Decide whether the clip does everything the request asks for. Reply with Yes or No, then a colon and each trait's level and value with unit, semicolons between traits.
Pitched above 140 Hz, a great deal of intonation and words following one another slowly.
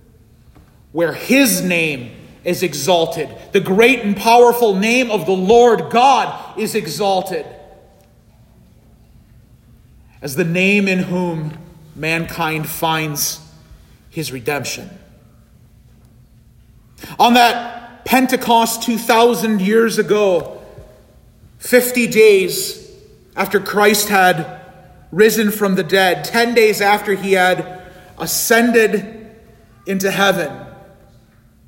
Yes: high, 190 Hz; wide, 5.9 semitones; slow, 90 wpm